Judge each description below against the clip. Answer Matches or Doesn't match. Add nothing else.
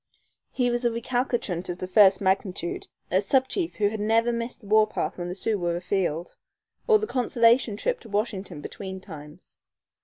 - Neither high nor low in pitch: Doesn't match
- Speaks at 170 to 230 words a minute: Matches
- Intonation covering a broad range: Doesn't match